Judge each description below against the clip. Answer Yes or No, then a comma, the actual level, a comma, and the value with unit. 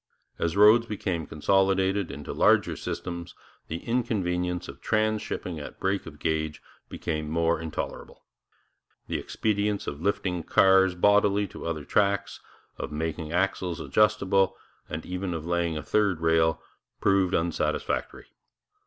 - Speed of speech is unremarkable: No, slow, 125 wpm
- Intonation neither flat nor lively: Yes, average, 3.4 semitones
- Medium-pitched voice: No, very low, 90 Hz